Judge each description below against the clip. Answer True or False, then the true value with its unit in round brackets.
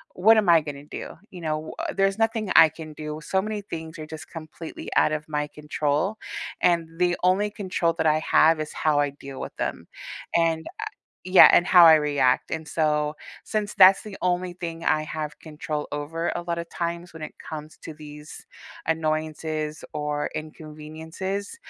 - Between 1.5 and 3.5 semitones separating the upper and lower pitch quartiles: True (2.7 semitones)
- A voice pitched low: False (160 Hz)